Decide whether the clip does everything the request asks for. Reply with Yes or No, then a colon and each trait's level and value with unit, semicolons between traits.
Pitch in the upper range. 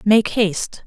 Yes: high, 205 Hz